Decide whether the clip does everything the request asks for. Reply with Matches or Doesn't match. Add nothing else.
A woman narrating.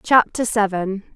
Matches